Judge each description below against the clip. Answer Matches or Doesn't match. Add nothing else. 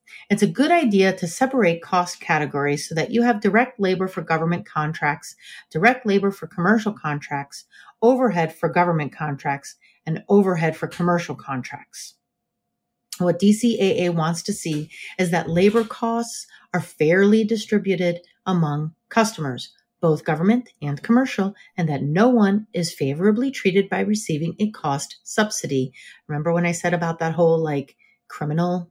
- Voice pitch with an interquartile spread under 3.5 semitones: Doesn't match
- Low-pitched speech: Doesn't match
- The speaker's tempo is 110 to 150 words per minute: Matches